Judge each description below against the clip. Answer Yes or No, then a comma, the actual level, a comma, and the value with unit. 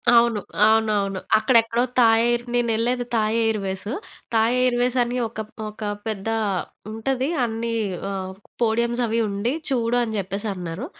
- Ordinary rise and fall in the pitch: No, narrow, 2.0 semitones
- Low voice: No, high, 225 Hz